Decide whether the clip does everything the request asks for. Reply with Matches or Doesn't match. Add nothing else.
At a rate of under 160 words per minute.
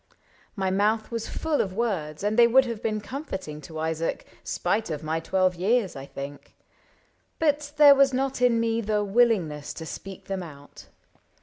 Doesn't match